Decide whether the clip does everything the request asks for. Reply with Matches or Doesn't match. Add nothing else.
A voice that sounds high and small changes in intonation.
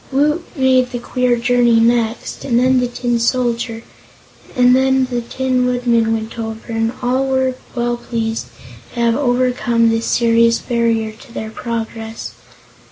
Matches